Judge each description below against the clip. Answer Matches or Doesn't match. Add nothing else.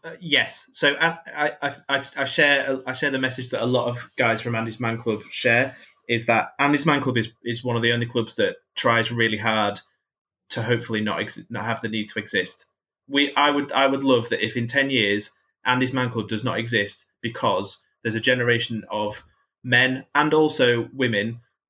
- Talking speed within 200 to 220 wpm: Matches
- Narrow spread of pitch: Doesn't match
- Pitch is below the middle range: Matches